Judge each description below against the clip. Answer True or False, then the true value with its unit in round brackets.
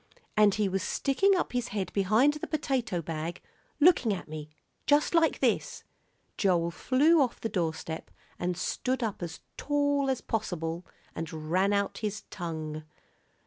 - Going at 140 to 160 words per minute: True (150 wpm)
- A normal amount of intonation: False (7.9 semitones)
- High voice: True (200 Hz)